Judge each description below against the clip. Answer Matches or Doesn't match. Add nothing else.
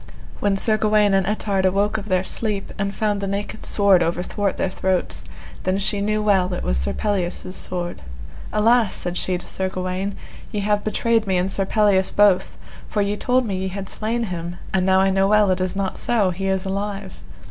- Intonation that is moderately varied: Doesn't match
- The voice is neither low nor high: Doesn't match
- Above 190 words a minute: Matches